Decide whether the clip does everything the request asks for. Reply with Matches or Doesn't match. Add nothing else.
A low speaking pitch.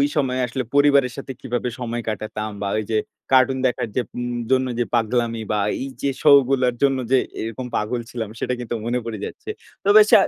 Matches